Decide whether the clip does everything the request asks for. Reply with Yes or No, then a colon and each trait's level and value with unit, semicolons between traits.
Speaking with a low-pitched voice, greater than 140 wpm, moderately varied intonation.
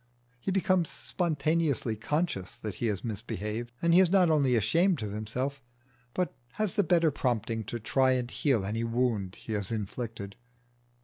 No: low, 125 Hz; average, 165 wpm; wide, 7.0 semitones